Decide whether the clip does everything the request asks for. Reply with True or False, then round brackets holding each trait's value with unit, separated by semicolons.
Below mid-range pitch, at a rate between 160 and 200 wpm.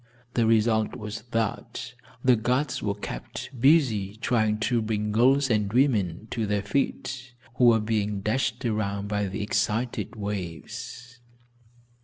False (110 Hz; 135 wpm)